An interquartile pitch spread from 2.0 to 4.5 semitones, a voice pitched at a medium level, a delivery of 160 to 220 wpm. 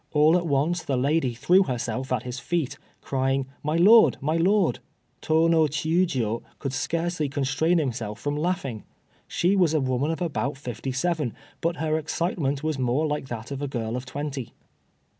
Yes: average, 4.1 semitones; medium, 145 Hz; average, 175 wpm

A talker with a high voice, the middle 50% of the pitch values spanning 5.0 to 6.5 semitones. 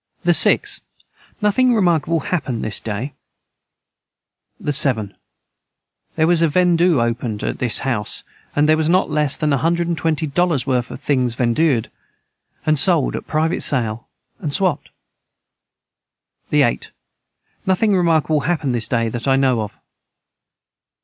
No: medium, 150 Hz; average, 5.3 semitones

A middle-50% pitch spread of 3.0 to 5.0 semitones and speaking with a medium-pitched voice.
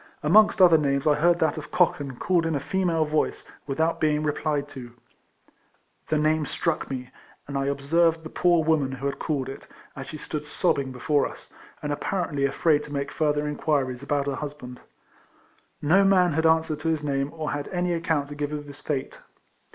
No: narrow, 2.4 semitones; medium, 150 Hz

